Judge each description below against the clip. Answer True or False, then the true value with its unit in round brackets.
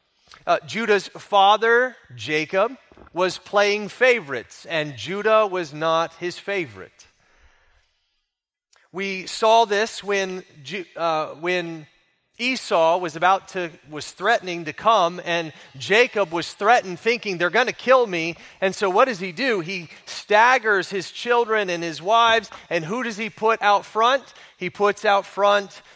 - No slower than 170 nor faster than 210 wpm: False (145 wpm)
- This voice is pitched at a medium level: False (195 Hz)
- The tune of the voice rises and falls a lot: False (4.4 semitones)